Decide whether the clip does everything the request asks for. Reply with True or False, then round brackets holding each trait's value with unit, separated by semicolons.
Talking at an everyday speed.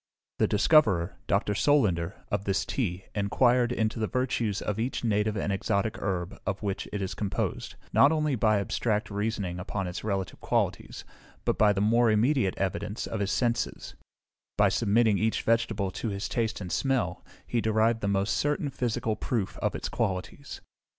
True (170 wpm)